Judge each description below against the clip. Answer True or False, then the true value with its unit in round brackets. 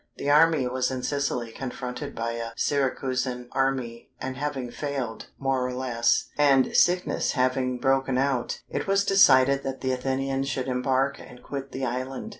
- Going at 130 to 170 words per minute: True (160 wpm)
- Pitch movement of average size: False (1.4 semitones)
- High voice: False (130 Hz)